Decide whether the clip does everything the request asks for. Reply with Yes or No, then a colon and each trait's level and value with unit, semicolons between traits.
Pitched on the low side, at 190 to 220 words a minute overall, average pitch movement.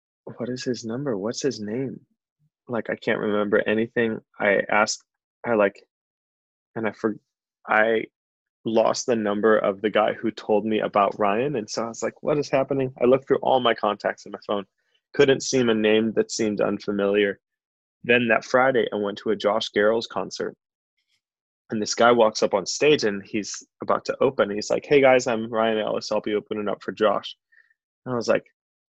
Yes: low, 110 Hz; average, 195 wpm; average, 3.4 semitones